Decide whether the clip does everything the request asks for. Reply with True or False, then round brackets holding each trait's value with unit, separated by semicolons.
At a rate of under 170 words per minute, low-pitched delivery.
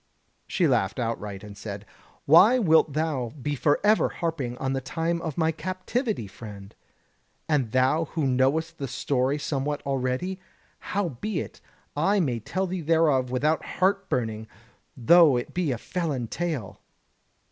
False (140 wpm; 145 Hz)